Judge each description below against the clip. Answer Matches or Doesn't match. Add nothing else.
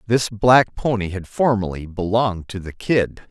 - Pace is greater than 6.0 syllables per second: Doesn't match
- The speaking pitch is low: Matches